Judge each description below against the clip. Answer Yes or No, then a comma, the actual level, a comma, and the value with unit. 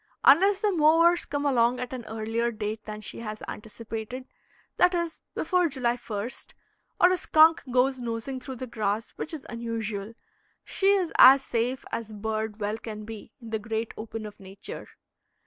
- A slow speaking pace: No, average, 170 wpm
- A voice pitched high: Yes, high, 235 Hz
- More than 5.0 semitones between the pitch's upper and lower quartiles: No, average, 4.2 semitones